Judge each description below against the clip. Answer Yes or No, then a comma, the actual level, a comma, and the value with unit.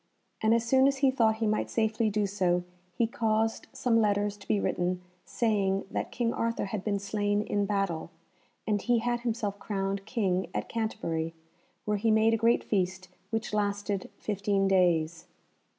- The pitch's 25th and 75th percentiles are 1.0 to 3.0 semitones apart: Yes, narrow, 2.6 semitones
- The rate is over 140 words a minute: Yes, average, 170 wpm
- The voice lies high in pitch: Yes, high, 210 Hz